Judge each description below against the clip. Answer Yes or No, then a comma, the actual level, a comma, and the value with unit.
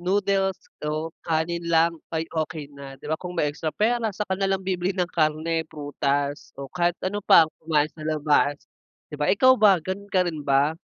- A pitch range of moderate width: Yes, average, 3.9 semitones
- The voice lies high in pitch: No, medium, 165 Hz